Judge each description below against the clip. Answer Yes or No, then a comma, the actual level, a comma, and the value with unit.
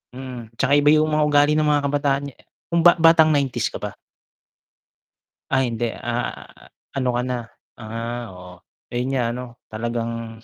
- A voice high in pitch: No, low, 130 Hz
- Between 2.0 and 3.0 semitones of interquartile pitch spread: No, average, 3.8 semitones